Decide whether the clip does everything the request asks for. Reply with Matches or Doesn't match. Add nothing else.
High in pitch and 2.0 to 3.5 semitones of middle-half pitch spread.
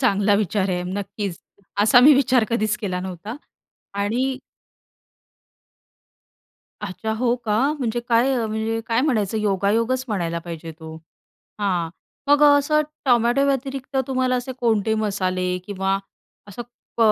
Doesn't match